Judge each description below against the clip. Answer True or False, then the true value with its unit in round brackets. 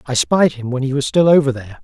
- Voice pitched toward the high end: False (135 Hz)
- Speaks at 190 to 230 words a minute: False (295 wpm)